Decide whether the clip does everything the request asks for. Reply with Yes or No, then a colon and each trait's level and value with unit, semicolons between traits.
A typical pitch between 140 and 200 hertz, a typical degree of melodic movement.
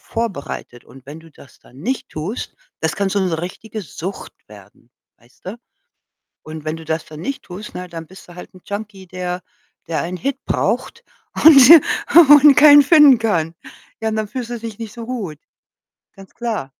No: high, 190 Hz; wide, 6.4 semitones